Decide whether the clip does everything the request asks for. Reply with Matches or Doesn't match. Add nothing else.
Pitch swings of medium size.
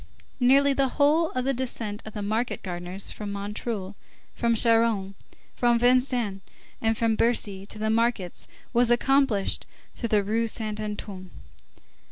Matches